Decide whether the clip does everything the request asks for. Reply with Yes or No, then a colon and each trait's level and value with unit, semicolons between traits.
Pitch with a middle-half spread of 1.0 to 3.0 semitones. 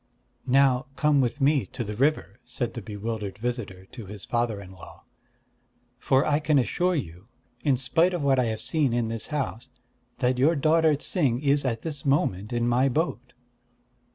No: average, 4.2 semitones